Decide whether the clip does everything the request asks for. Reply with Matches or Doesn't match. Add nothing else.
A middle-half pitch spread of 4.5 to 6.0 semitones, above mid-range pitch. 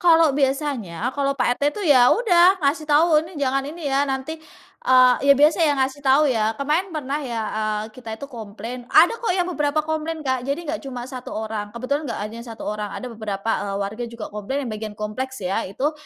Matches